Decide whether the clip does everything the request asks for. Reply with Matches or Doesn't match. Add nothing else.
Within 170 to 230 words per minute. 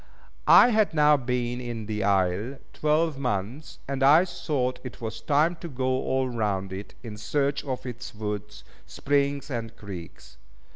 Doesn't match